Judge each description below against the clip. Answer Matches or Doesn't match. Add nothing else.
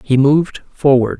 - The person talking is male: Matches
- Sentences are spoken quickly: Doesn't match